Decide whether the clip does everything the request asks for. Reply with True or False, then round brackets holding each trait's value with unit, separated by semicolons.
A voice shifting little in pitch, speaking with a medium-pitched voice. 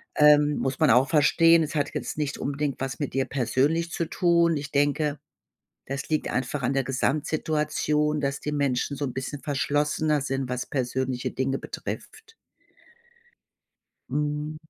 True (2.0 semitones; 145 Hz)